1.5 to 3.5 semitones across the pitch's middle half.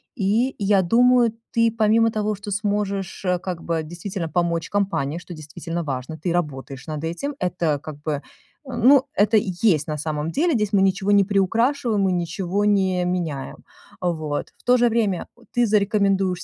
No: average, 4.2 semitones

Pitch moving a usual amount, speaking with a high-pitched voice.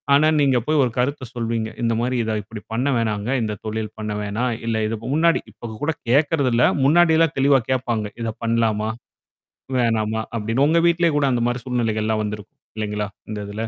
No: average, 3.9 semitones; low, 115 Hz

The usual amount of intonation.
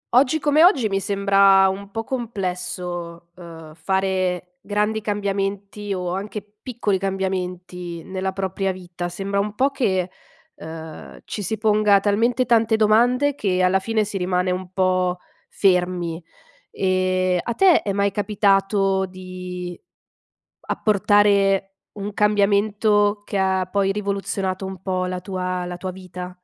No: narrow, 2.1 semitones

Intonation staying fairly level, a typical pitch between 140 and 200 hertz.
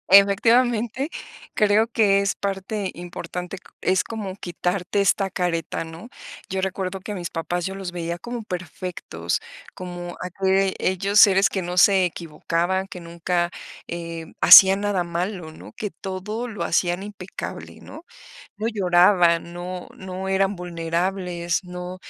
Yes: narrow, 2.2 semitones; medium, 185 Hz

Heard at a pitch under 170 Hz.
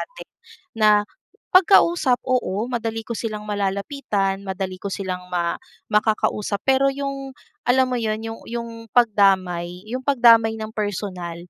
No: high, 215 Hz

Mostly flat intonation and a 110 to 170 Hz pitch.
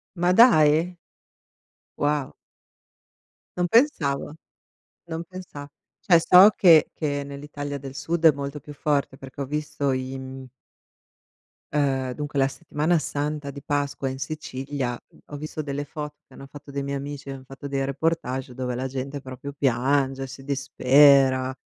Yes: narrow, 2.0 semitones; medium, 140 Hz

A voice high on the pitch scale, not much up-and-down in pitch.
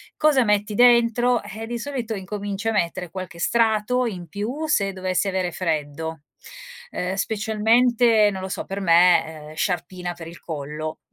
No: high, 200 Hz; average, 4.3 semitones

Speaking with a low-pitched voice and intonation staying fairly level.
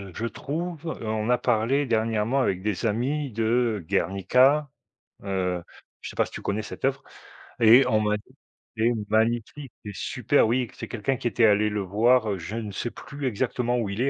No: low, 115 Hz; average, 3.3 semitones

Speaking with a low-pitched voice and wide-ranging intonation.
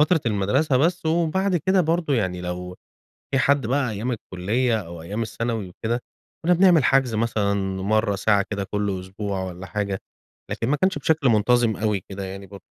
Yes: low, 110 Hz; wide, 6.0 semitones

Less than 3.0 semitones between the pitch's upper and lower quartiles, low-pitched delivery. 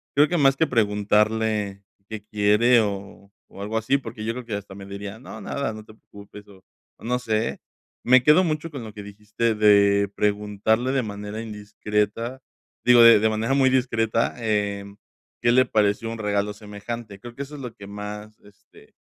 Yes: narrow, 2.5 semitones; low, 110 Hz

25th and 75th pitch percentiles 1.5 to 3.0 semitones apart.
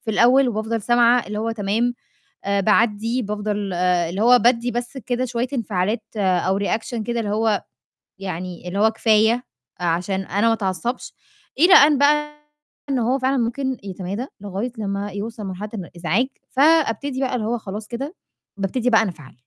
No: average, 3.6 semitones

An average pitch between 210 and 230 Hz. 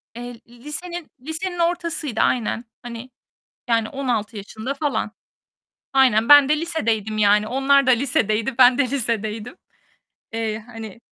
No: high, 245 Hz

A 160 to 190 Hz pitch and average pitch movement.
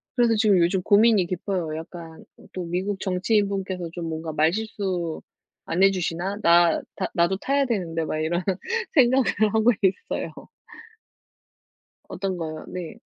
Yes: medium, 185 Hz; average, 3.3 semitones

